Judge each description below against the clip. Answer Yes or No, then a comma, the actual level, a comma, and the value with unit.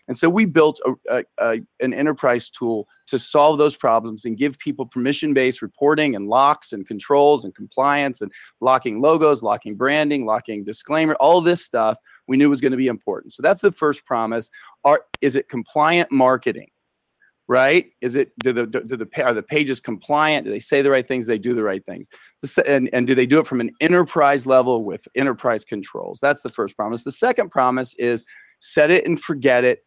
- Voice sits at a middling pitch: No, low, 130 Hz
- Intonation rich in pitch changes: No, average, 3.8 semitones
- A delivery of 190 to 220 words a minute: Yes, fast, 205 wpm